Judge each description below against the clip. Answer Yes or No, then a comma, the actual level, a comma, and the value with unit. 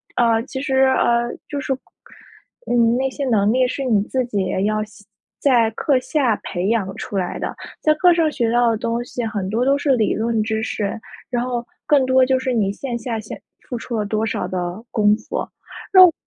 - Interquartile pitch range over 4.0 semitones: No, average, 3.3 semitones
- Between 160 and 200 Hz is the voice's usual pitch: No, high, 235 Hz